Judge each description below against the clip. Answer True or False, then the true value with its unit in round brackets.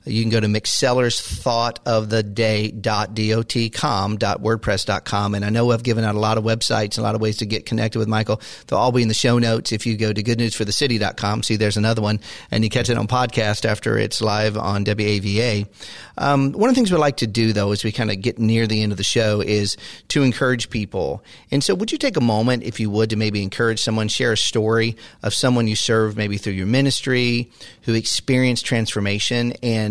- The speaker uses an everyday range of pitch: False (2.0 semitones)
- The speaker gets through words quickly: True (210 wpm)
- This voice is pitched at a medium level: False (110 Hz)